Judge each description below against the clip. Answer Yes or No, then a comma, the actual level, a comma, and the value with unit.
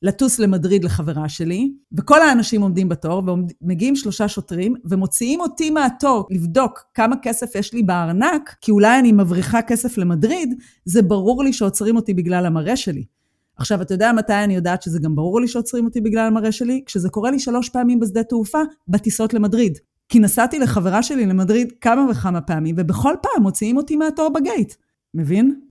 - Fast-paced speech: Yes, fast, 170 wpm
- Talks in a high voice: Yes, high, 220 Hz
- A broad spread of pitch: No, average, 4.8 semitones